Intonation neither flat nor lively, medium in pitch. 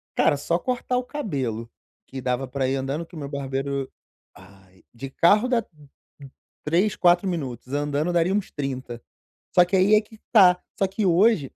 No: wide, 6.3 semitones; medium, 155 Hz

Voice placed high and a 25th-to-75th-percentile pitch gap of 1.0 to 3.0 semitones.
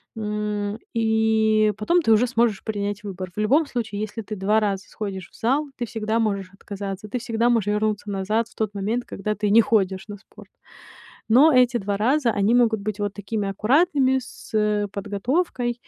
Yes: high, 215 Hz; narrow, 2.4 semitones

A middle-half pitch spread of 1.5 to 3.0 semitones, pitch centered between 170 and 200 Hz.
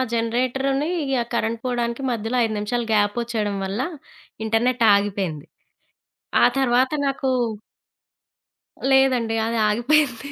No: average, 2.7 semitones; high, 235 Hz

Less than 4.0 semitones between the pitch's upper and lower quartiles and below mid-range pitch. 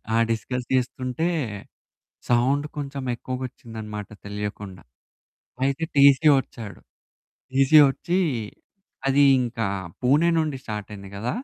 No: average, 4.3 semitones; low, 125 Hz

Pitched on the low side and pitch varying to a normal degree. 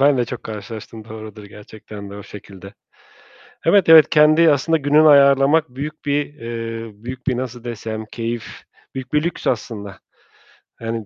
Yes: low, 120 Hz; average, 4.9 semitones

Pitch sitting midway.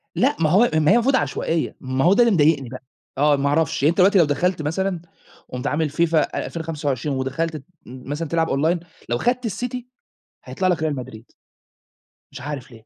Yes: medium, 155 Hz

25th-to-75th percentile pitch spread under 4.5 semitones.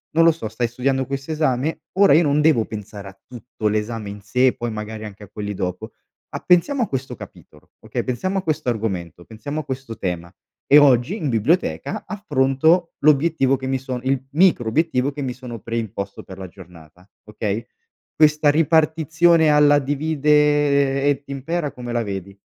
No: wide, 5.7 semitones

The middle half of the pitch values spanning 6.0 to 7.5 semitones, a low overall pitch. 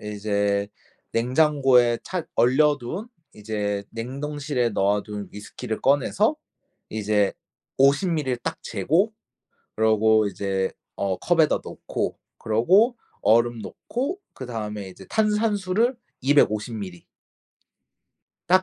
Yes: wide, 6.7 semitones; low, 120 Hz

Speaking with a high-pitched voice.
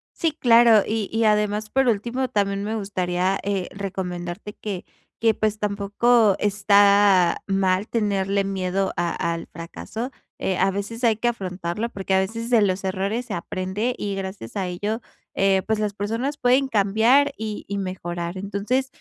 Yes: high, 200 Hz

